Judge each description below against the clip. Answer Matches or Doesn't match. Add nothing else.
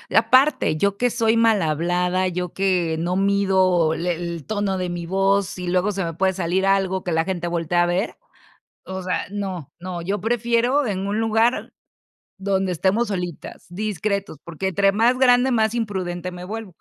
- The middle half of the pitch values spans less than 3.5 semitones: Matches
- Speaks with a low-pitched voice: Doesn't match